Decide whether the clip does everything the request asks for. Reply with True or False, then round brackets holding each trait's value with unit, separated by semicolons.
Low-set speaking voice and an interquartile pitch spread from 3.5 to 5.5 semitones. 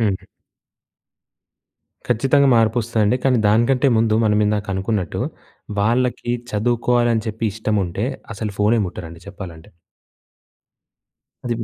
False (110 Hz; 2.6 semitones)